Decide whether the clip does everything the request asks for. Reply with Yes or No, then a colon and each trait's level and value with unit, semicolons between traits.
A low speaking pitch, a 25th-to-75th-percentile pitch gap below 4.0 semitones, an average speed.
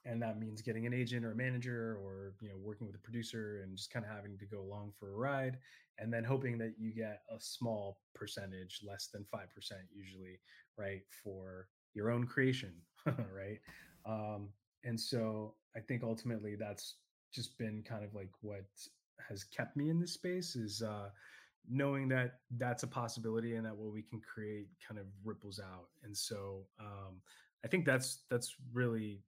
Yes: low, 110 Hz; average, 3.2 semitones; average, 185 wpm